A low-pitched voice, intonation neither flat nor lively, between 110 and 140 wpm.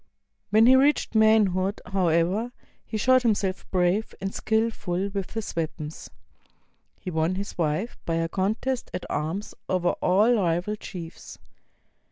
No: high, 195 Hz; average, 3.8 semitones; slow, 135 wpm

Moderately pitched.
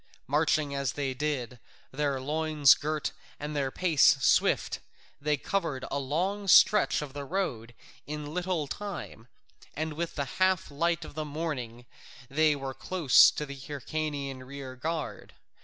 Yes: medium, 150 Hz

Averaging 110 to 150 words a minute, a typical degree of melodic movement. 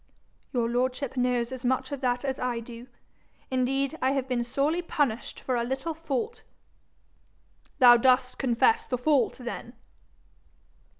No: average, 140 wpm; narrow, 2.1 semitones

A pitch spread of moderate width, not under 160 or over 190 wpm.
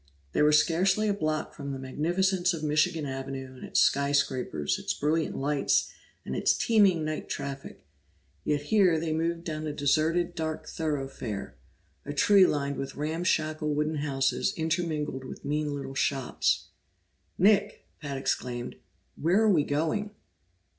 No: average, 3.2 semitones; average, 145 wpm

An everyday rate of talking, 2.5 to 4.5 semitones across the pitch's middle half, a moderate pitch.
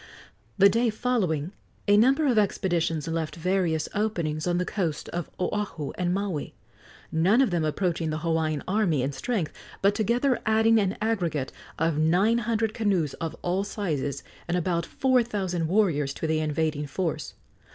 No: average, 160 wpm; average, 5.0 semitones; medium, 180 Hz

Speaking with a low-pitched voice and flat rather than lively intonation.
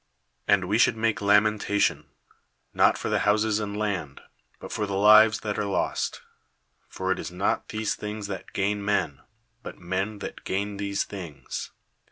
Yes: low, 100 Hz; narrow, 1.7 semitones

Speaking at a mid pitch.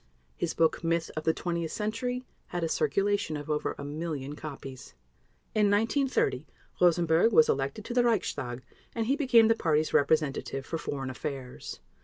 Yes: medium, 165 Hz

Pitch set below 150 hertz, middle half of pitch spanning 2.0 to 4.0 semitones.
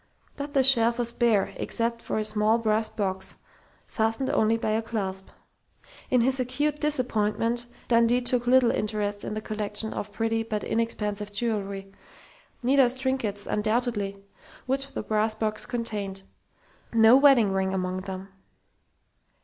No: high, 225 Hz; narrow, 2.6 semitones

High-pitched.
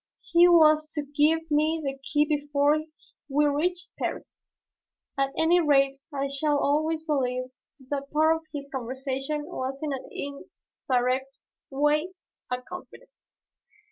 Yes: very high, 290 Hz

